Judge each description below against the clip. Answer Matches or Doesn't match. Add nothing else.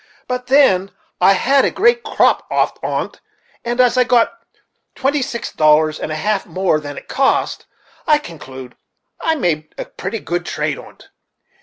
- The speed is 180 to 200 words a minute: Doesn't match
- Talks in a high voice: Matches